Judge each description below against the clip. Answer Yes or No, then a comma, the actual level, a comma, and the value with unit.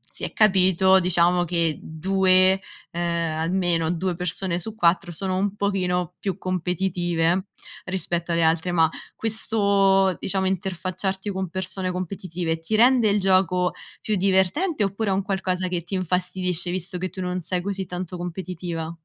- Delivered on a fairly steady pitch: Yes, narrow, 1.7 semitones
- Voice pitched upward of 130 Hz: Yes, medium, 185 Hz